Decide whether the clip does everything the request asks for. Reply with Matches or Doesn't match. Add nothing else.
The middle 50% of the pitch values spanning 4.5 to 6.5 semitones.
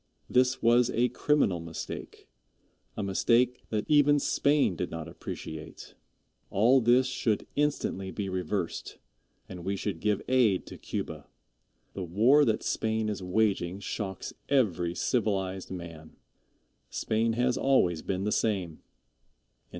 Matches